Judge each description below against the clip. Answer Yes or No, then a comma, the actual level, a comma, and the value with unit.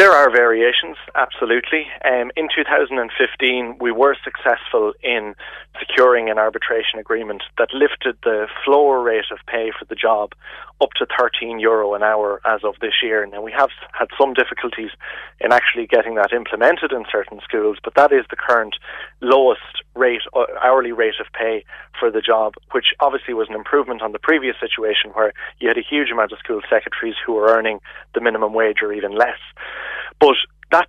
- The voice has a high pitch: No, medium, 140 Hz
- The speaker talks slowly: No, average, 180 wpm